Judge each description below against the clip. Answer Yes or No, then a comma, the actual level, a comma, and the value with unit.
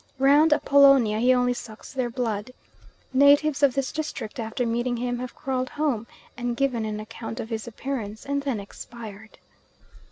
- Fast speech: No, average, 160 wpm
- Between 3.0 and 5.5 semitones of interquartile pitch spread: Yes, average, 3.5 semitones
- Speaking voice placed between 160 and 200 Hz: No, high, 245 Hz